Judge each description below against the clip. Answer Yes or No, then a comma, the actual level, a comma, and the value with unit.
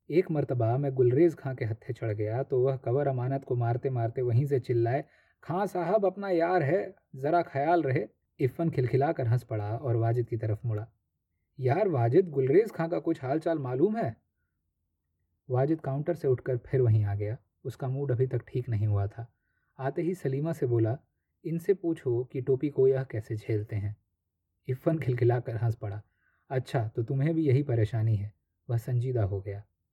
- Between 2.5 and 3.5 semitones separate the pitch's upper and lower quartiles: No, average, 4.2 semitones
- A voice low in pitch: Yes, low, 125 Hz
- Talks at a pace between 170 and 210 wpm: Yes, average, 185 wpm